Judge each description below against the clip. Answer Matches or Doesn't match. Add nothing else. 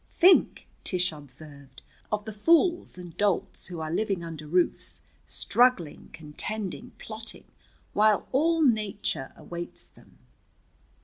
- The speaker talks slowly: Matches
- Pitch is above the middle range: Matches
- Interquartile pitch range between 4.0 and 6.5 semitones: Matches